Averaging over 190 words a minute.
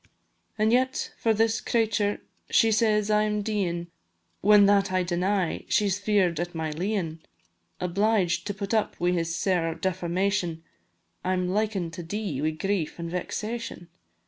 No: average, 150 wpm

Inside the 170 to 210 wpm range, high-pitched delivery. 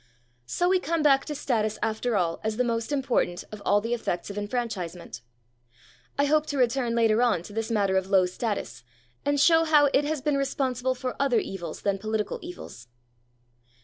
Yes: average, 185 wpm; high, 235 Hz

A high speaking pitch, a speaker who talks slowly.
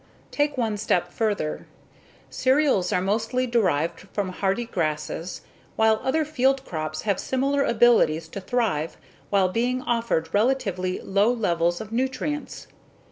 Yes: high, 215 Hz; slow, 130 wpm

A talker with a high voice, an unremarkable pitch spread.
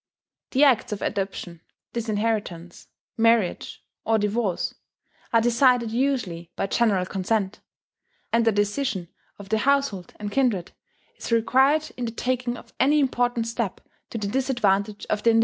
Yes: high, 225 Hz; average, 3.5 semitones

